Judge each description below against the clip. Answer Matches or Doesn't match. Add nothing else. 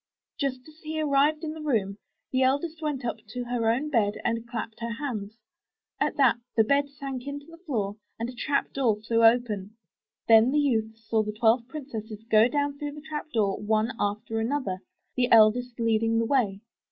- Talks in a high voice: Matches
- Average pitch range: Matches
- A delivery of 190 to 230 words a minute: Matches